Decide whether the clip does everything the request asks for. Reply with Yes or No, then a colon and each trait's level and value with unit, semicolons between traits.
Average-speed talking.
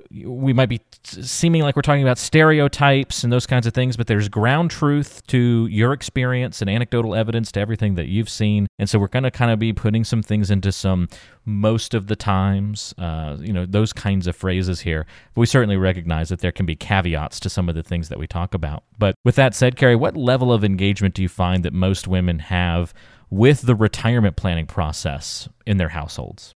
No: fast, 215 wpm